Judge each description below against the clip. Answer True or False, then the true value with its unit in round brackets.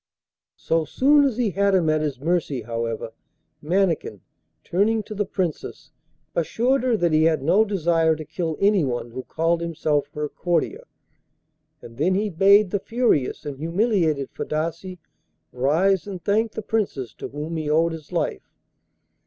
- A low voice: False (170 Hz)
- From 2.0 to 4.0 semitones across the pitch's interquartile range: False (4.9 semitones)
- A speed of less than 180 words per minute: True (155 wpm)